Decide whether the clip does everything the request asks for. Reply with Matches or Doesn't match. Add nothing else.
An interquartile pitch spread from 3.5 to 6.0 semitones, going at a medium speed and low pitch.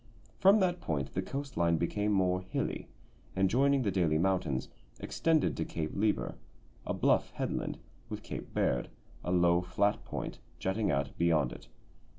Matches